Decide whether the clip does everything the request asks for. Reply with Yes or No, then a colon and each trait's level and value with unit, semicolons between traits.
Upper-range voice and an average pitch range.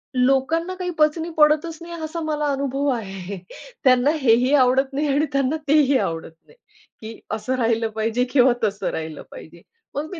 Yes: very high, 270 Hz; average, 4.9 semitones